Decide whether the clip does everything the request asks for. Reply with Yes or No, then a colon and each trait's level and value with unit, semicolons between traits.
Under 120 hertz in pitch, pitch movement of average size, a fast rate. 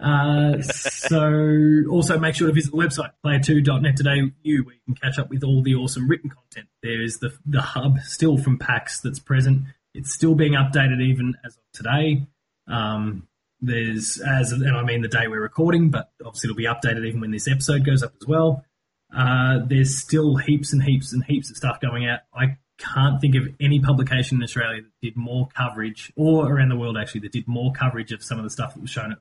No: low, 135 Hz; average, 3.1 semitones; fast, 220 wpm